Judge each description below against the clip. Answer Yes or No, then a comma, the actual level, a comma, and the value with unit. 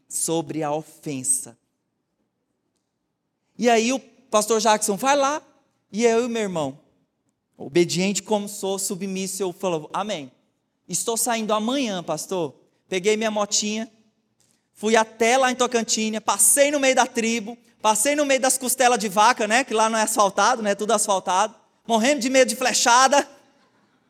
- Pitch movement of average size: Yes, average, 4.1 semitones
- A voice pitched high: Yes, high, 220 Hz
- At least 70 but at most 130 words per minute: No, average, 150 wpm